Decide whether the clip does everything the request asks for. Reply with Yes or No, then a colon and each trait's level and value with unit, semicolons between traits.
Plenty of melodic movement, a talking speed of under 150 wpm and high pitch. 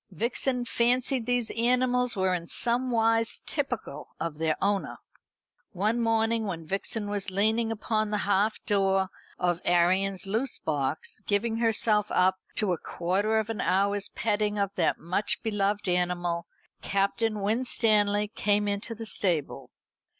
No: average, 3.1 semitones; average, 140 wpm; high, 205 Hz